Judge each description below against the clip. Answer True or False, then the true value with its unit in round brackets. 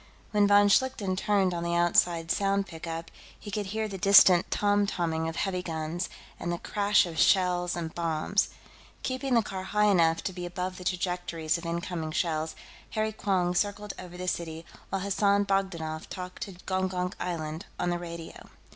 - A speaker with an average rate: True (175 wpm)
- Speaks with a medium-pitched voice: True (180 Hz)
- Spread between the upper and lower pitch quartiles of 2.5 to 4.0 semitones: True (2.9 semitones)